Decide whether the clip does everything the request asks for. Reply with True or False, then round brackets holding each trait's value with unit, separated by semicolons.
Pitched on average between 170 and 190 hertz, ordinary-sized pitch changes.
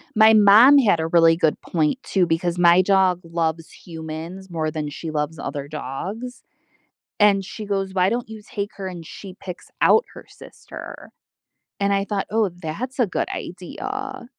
True (185 Hz; 4.1 semitones)